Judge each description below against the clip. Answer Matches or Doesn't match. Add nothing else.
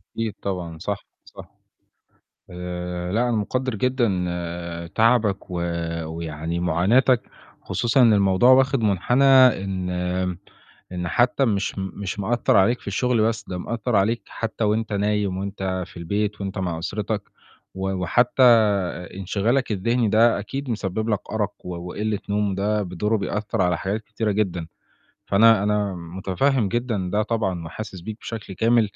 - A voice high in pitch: Doesn't match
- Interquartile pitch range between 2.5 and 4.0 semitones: Matches